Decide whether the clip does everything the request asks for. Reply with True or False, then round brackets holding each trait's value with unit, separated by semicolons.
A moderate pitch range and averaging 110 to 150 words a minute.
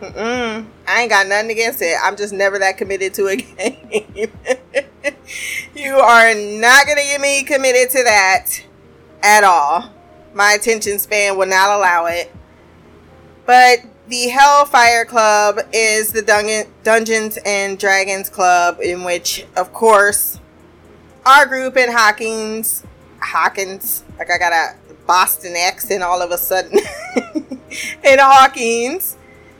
True (4.6 semitones; 135 wpm)